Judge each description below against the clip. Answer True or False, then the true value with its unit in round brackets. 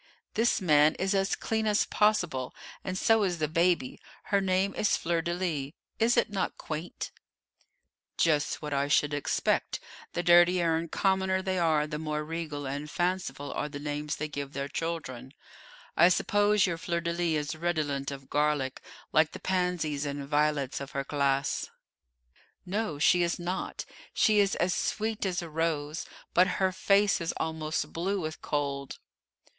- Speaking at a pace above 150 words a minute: True (165 wpm)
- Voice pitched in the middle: True (165 Hz)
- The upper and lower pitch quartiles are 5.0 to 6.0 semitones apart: False (4.1 semitones)